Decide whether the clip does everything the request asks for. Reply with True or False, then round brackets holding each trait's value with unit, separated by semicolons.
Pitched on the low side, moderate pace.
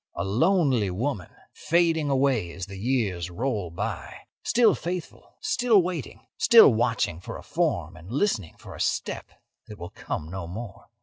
True (115 Hz; 160 wpm)